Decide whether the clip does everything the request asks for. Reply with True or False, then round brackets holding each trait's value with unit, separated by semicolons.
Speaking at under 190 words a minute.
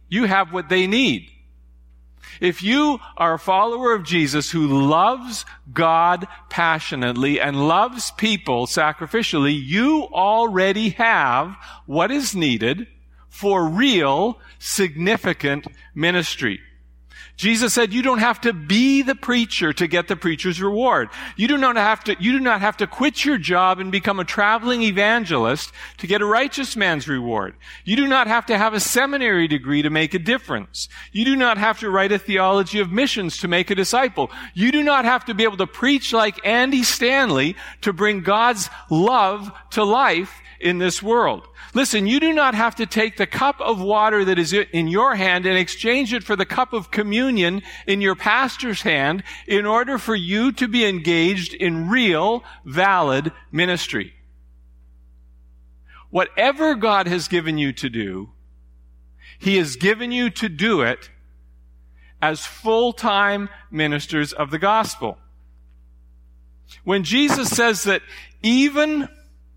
True (155 wpm)